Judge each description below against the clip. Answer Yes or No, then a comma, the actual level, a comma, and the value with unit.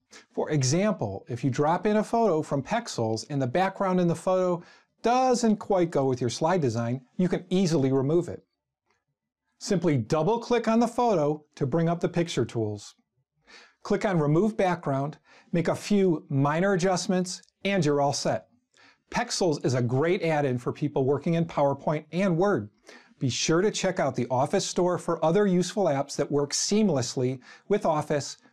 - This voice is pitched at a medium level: Yes, medium, 165 Hz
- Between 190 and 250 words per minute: No, average, 175 wpm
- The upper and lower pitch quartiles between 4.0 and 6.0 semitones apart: Yes, wide, 5.4 semitones